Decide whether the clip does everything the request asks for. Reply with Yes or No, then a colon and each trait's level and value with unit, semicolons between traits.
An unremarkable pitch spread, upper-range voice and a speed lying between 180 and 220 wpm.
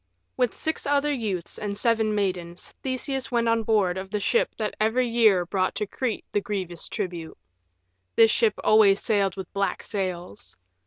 No: average, 3.3 semitones; high, 210 Hz; average, 165 wpm